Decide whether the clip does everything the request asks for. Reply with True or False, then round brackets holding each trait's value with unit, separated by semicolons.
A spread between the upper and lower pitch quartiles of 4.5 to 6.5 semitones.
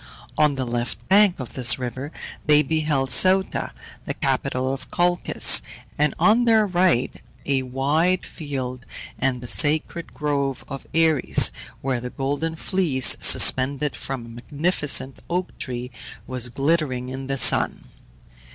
False (4.0 semitones)